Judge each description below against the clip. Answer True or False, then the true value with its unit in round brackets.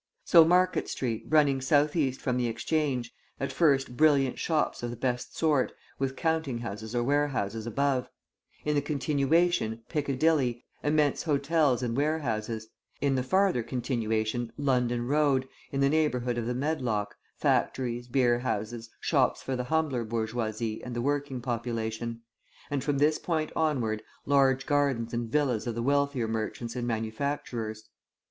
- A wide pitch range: False (3.7 semitones)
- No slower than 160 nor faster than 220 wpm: False (145 wpm)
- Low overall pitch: True (130 Hz)